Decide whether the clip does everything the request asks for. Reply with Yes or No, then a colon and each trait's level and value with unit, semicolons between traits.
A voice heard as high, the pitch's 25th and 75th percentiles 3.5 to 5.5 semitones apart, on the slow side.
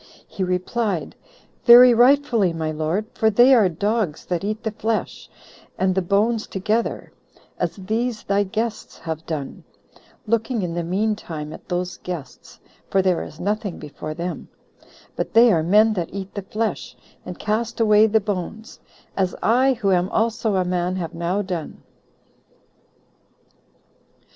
No: high, 200 Hz; average, 3.9 semitones; average, 150 wpm